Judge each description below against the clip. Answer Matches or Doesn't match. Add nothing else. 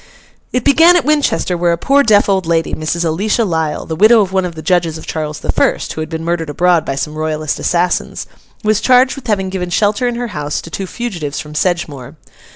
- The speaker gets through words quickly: Matches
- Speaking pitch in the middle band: Matches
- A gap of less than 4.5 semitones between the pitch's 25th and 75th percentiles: Doesn't match